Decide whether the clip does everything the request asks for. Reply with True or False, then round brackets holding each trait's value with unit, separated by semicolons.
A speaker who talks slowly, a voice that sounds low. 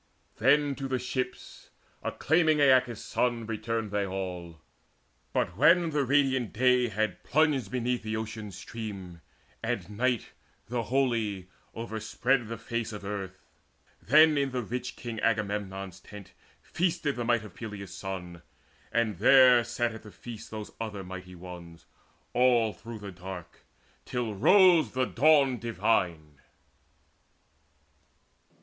True (130 wpm; 115 Hz)